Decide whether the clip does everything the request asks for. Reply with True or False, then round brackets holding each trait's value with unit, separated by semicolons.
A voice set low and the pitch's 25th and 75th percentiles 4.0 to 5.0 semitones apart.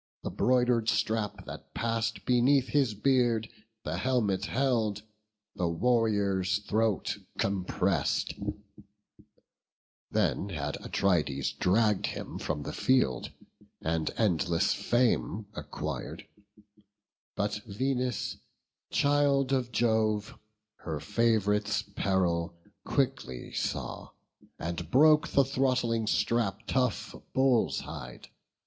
True (110 Hz; 4.5 semitones)